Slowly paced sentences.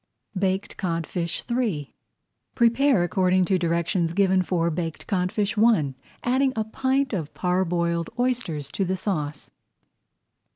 Yes: slow, 120 wpm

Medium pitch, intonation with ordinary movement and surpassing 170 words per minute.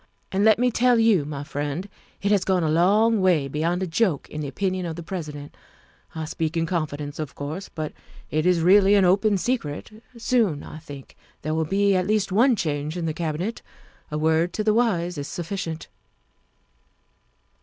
Yes: medium, 175 Hz; average, 4.7 semitones; average, 185 wpm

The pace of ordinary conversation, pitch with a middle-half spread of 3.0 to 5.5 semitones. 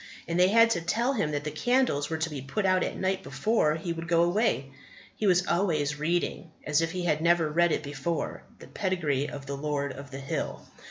No: fast, 225 wpm; average, 4.0 semitones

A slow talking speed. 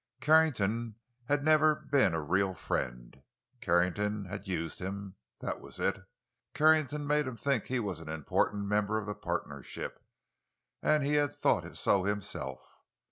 No: average, 145 wpm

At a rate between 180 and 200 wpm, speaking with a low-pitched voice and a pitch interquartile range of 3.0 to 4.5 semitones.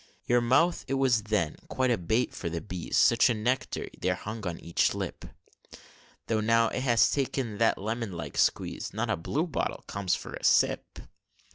Yes: average, 185 wpm; low, 115 Hz; average, 3.9 semitones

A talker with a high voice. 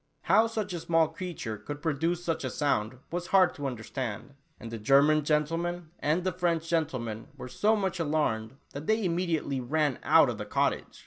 No: medium, 155 Hz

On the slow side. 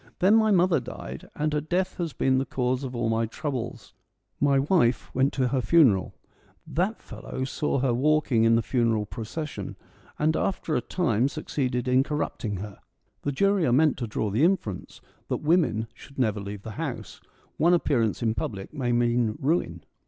No: average, 180 wpm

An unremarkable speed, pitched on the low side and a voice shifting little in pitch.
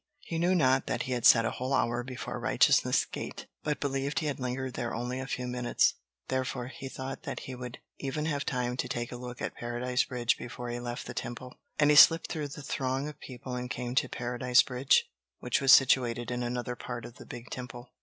No: fast, 225 wpm; low, 125 Hz; narrow, 1.6 semitones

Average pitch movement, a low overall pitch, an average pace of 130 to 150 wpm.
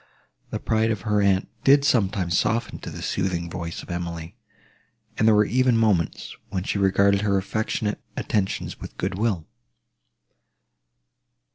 Yes: average, 3.1 semitones; low, 100 Hz; average, 140 wpm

